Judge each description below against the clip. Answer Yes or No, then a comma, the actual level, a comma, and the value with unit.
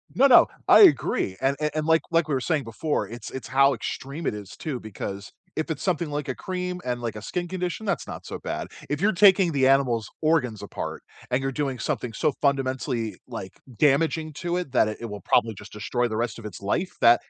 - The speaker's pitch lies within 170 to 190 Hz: No, low, 135 Hz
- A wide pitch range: Yes, wide, 5.9 semitones